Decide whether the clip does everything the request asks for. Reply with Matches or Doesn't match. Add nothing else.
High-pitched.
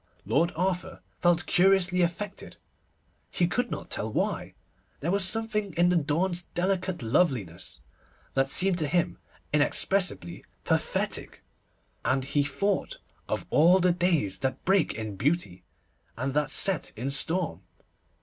Doesn't match